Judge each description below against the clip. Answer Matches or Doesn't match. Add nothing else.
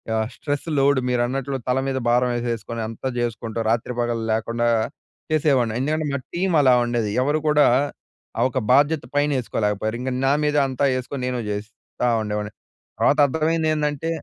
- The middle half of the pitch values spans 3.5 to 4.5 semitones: Matches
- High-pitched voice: Doesn't match